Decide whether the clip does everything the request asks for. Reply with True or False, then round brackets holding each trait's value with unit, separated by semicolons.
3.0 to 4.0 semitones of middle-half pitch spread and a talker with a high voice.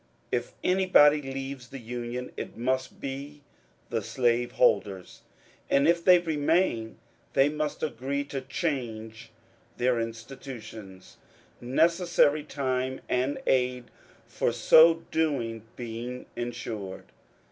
False (3.7 semitones; 130 Hz)